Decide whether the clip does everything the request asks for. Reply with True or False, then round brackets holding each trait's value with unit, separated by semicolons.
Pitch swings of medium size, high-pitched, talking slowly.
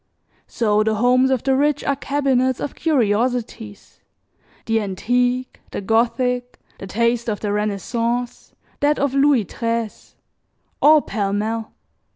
True (3.2 semitones; 240 Hz; 130 wpm)